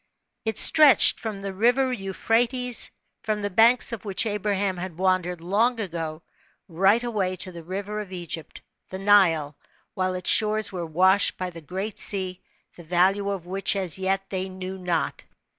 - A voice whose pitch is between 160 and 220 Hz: Yes, high, 190 Hz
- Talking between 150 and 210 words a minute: Yes, average, 165 wpm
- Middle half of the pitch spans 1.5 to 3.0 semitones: Yes, narrow, 2.5 semitones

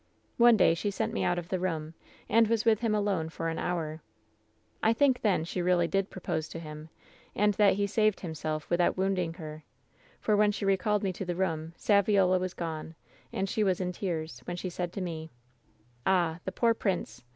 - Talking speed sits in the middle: No, fast, 215 wpm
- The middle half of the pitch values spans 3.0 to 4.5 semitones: Yes, average, 3.8 semitones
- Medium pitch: Yes, medium, 180 Hz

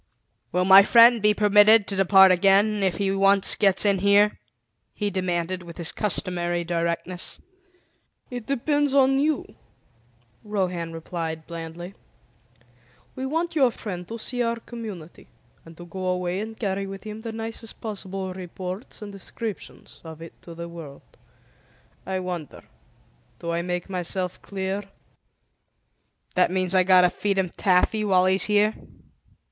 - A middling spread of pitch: Yes, average, 3.0 semitones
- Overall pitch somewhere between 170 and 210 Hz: Yes, high, 190 Hz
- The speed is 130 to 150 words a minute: Yes, average, 145 wpm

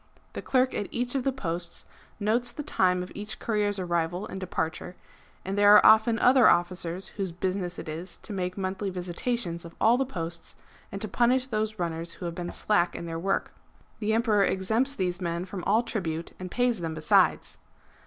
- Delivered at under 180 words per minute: No, average, 195 wpm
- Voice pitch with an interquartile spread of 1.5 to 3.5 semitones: No, average, 4.1 semitones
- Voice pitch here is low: No, high, 190 Hz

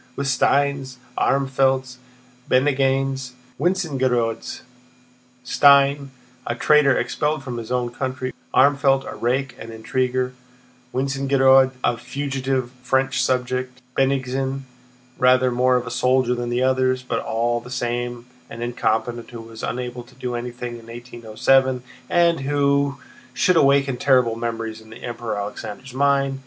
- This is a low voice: Yes, low, 130 Hz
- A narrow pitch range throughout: Yes, narrow, 2.0 semitones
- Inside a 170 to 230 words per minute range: No, slow, 135 wpm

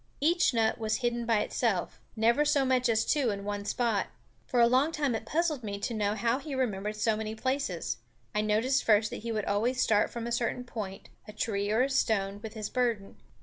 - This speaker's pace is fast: Yes, fast, 220 wpm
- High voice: Yes, high, 225 Hz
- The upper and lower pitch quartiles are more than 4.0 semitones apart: No, average, 3.2 semitones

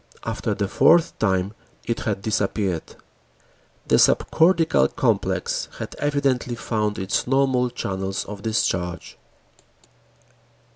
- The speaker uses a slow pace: Yes, slow, 100 wpm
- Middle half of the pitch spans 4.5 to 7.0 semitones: Yes, average, 5.0 semitones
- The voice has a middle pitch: No, low, 110 Hz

